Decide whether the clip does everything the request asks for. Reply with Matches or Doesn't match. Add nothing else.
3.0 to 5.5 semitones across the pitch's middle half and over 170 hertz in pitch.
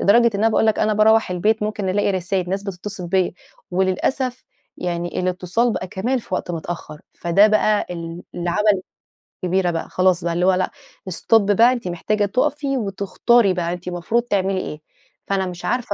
Matches